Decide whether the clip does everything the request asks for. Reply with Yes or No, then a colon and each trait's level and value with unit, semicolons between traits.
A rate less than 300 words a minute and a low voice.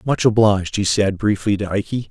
Yes: average, 200 wpm; low, 105 Hz